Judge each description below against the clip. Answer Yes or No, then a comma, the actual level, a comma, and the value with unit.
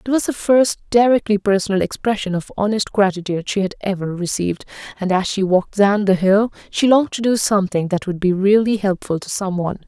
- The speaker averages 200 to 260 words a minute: Yes, fast, 205 wpm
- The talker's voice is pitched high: Yes, high, 200 Hz